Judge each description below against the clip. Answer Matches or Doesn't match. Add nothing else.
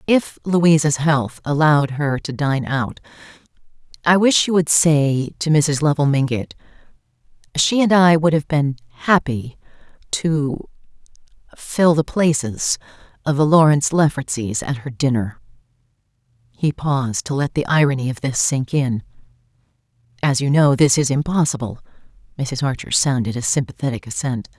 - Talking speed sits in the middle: Doesn't match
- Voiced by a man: Doesn't match